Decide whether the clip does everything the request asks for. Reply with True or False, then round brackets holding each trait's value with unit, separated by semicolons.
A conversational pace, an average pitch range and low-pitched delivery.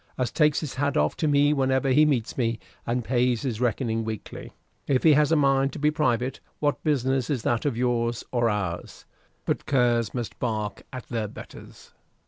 True (190 wpm; 3.4 semitones; 125 Hz)